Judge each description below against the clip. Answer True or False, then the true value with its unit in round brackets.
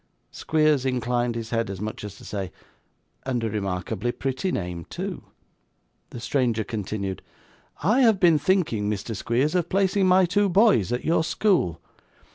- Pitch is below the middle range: True (120 Hz)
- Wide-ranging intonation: True (8.9 semitones)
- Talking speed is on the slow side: False (155 wpm)